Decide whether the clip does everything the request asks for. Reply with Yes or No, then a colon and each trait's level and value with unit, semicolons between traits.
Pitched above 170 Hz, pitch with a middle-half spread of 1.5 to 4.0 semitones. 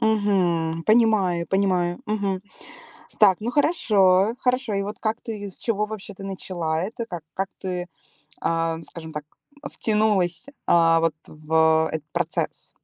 No: high, 190 Hz; average, 4.4 semitones